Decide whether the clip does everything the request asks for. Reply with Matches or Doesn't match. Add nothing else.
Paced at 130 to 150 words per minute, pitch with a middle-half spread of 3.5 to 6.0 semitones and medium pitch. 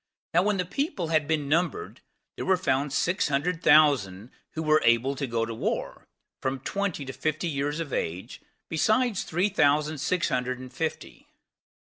Doesn't match